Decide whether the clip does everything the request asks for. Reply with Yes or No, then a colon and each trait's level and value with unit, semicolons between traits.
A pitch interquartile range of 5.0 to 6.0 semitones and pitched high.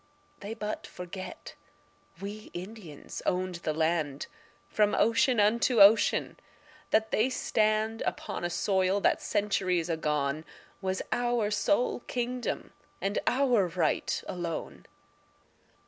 No: average, 4.3 semitones; high, 200 Hz